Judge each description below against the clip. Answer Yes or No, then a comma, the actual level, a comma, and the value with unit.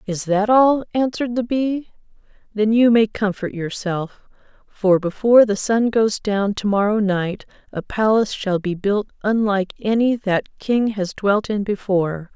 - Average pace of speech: Yes, average, 160 wpm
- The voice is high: Yes, high, 210 Hz